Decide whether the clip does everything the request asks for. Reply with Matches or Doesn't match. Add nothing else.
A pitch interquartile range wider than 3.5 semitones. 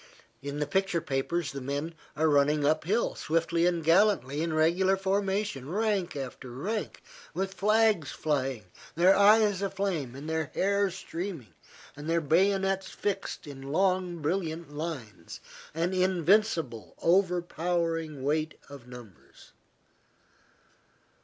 Matches